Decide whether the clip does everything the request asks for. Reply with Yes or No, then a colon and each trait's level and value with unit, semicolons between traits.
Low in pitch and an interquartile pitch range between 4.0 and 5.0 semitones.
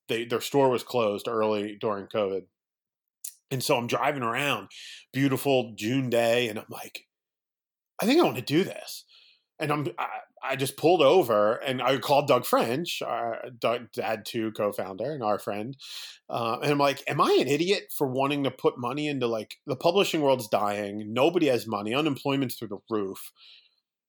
Yes: low, 125 Hz; average, 4.4 semitones